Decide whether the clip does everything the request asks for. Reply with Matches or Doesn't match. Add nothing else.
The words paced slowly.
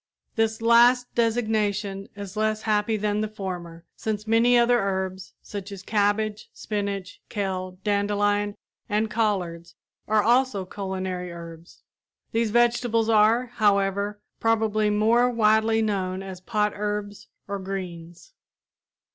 Matches